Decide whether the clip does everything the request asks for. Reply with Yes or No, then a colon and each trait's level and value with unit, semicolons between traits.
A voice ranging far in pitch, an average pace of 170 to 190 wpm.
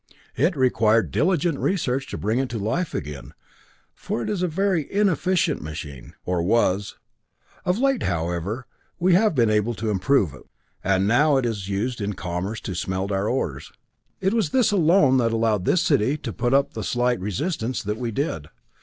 Yes: wide, 7.9 semitones; average, 180 wpm